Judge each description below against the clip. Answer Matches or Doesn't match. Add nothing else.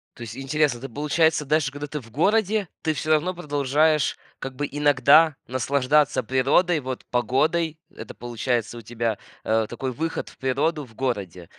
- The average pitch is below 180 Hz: Matches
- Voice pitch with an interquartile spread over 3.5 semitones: Matches